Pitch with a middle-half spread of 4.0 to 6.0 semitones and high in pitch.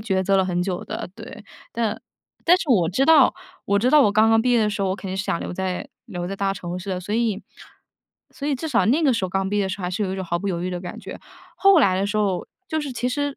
Yes: average, 4.5 semitones; high, 200 Hz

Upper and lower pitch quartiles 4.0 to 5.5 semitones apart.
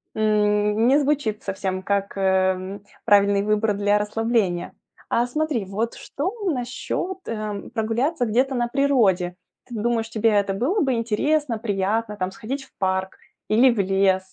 No: average, 3.6 semitones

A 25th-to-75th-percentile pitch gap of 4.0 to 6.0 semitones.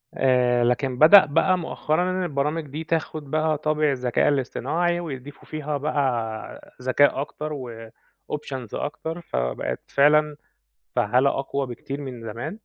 No: average, 3.3 semitones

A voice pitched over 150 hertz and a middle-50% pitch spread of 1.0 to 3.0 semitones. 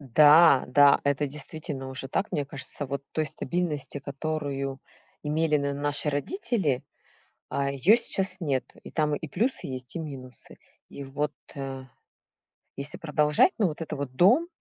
No: medium, 145 Hz; narrow, 2.4 semitones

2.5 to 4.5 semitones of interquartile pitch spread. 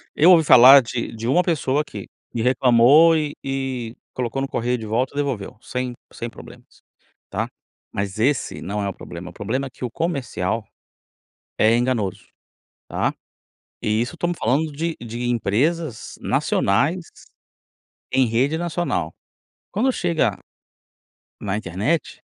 No: average, 4.9 semitones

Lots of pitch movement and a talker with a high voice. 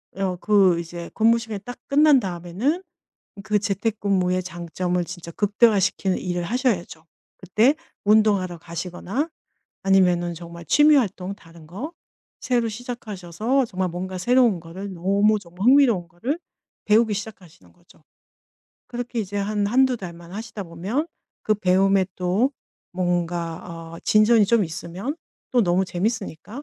No: average, 4.3 semitones; high, 195 Hz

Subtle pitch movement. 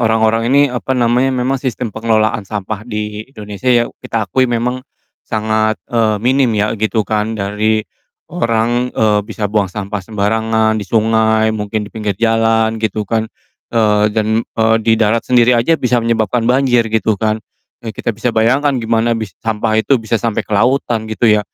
Yes: narrow, 1.6 semitones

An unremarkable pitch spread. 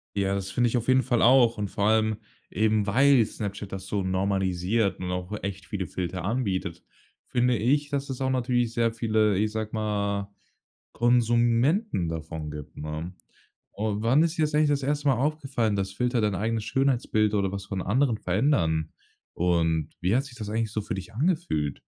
Yes: average, 4.4 semitones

